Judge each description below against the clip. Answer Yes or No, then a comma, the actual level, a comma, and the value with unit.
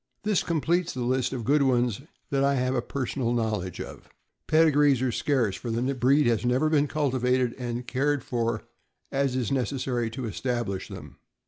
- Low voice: Yes, low, 130 Hz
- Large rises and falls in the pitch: No, average, 2.8 semitones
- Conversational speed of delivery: Yes, average, 175 wpm